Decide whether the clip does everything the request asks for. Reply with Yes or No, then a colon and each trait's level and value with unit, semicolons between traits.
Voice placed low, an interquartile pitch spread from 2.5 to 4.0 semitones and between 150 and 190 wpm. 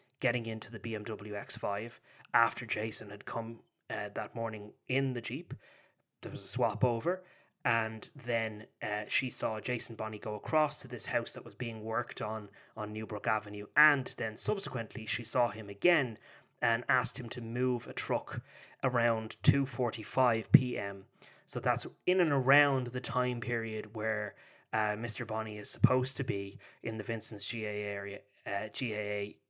Yes: low, 115 Hz; average, 2.8 semitones; average, 175 wpm